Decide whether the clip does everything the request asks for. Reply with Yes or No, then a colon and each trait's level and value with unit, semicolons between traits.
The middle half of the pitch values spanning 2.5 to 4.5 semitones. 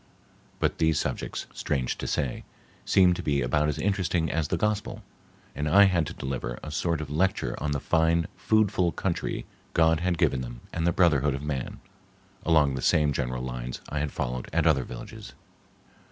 Yes: average, 3.9 semitones